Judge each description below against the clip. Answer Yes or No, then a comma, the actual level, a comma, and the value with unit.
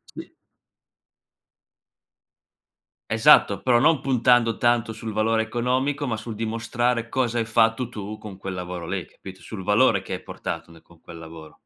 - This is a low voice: Yes, low, 115 Hz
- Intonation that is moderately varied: Yes, average, 3.7 semitones